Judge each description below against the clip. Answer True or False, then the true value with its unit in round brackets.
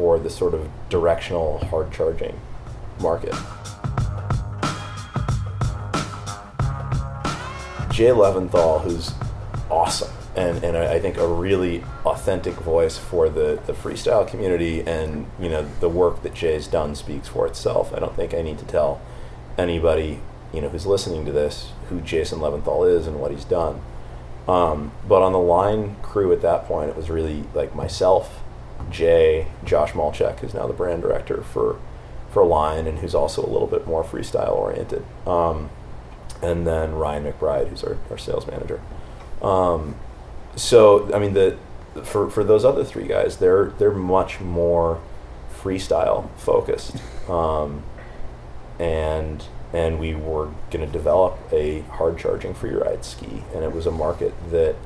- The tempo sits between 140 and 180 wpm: True (150 wpm)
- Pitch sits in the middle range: False (105 Hz)